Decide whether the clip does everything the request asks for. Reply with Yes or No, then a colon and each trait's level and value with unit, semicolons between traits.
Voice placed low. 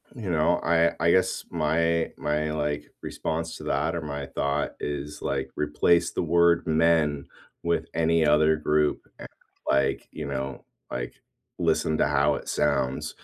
Yes: very low, 75 Hz